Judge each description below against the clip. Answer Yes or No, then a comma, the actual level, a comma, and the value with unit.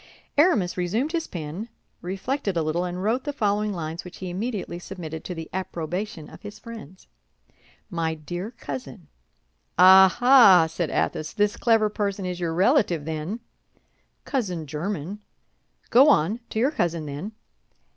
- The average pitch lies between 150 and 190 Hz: Yes, medium, 185 Hz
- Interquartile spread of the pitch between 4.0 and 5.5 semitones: Yes, average, 4.8 semitones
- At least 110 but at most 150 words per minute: Yes, average, 145 wpm